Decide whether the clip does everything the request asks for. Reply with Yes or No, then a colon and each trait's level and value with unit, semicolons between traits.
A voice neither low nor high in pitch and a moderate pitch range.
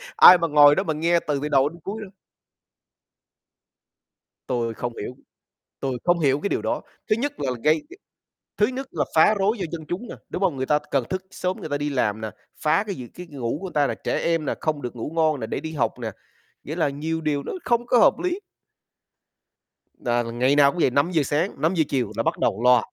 Yes: medium, 150 Hz; average, 5.0 semitones